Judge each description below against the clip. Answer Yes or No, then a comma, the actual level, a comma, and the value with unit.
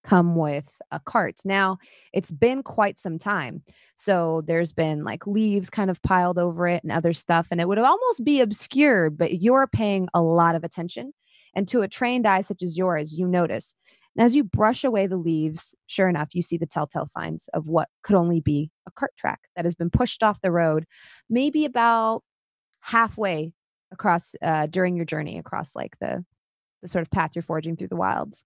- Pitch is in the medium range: Yes, medium, 180 Hz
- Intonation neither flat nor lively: Yes, average, 4.1 semitones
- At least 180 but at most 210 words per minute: Yes, average, 200 wpm